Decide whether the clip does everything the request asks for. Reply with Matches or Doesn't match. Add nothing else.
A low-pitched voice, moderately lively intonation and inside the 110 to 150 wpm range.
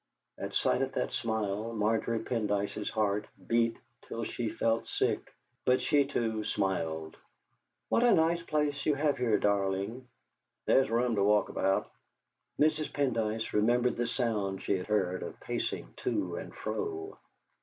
Matches